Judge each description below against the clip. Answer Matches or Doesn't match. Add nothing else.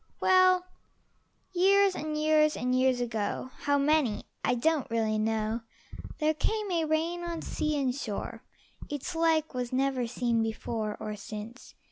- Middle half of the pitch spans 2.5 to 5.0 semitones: Doesn't match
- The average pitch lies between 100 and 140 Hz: Doesn't match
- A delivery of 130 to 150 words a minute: Matches